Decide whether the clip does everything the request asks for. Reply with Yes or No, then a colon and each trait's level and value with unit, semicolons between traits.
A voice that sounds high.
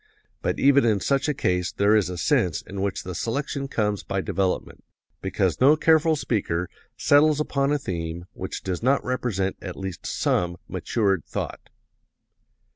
No: low, 105 Hz